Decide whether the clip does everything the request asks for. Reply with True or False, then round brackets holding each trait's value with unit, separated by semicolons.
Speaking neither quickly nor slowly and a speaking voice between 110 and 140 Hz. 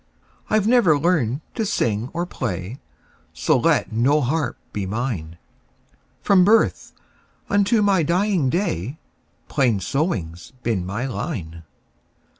False (110 wpm; 135 Hz)